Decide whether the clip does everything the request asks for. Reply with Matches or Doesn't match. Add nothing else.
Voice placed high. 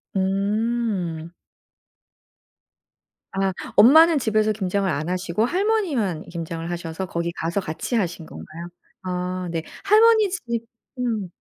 Matches